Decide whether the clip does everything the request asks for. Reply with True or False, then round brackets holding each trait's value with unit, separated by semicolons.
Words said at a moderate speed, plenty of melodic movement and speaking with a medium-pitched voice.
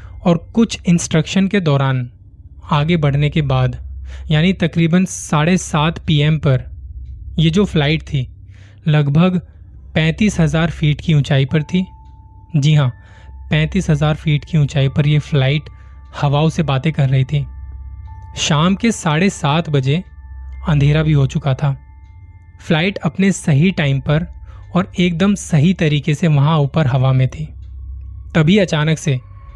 True (145 wpm; 8.8 semitones; 150 Hz)